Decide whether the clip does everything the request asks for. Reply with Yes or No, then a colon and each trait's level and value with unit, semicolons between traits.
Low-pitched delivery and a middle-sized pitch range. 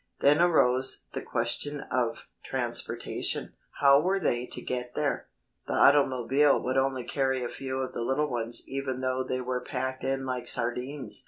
No: low, 130 Hz; narrow, 1.7 semitones